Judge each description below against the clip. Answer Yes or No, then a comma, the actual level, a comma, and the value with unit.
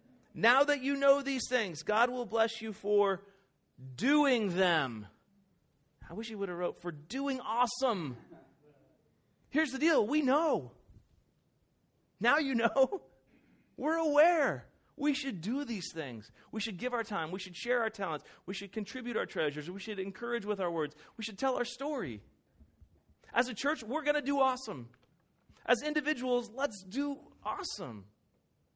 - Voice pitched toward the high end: Yes, high, 230 Hz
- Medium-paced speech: Yes, average, 160 wpm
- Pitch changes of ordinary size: No, wide, 6.4 semitones